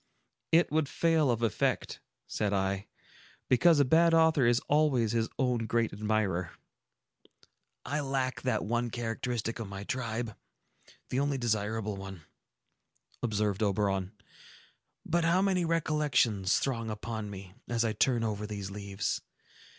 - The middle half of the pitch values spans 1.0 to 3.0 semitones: No, average, 4.7 semitones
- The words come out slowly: Yes, slow, 130 wpm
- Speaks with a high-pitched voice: No, low, 115 Hz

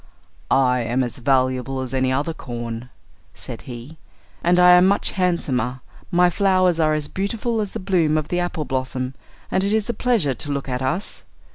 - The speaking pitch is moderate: Yes, medium, 150 Hz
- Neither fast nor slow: Yes, average, 185 wpm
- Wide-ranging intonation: Yes, wide, 5.8 semitones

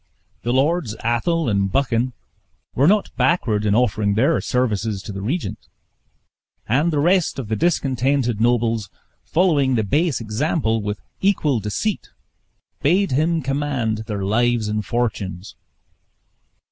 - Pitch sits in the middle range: No, low, 120 Hz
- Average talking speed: No, slow, 130 wpm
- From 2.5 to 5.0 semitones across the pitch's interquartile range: No, wide, 5.5 semitones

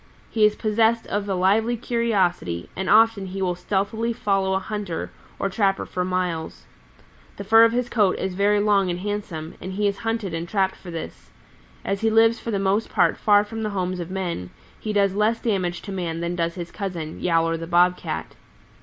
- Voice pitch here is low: No, high, 195 Hz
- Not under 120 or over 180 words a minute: No, fast, 205 wpm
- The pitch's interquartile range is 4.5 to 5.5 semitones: No, average, 3.0 semitones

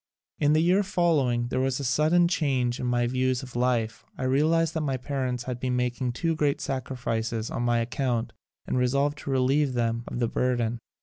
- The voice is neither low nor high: No, low, 130 Hz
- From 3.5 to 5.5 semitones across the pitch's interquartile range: No, average, 3.1 semitones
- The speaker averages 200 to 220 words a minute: Yes, fast, 205 wpm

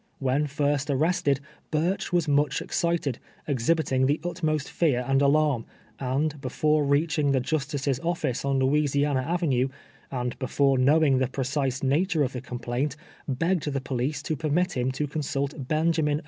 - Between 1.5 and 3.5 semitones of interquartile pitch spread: Yes, average, 2.7 semitones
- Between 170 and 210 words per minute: No, average, 155 wpm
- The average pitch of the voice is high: No, medium, 145 Hz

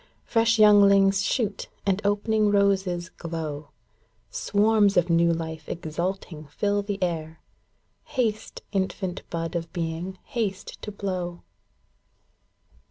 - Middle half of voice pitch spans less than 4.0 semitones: Yes, average, 3.4 semitones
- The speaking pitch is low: No, high, 190 Hz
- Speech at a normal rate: No, slow, 110 wpm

